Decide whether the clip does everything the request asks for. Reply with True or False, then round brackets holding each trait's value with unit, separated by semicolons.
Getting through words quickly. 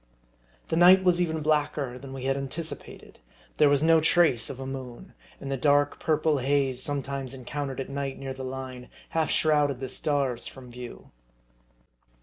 False (165 wpm)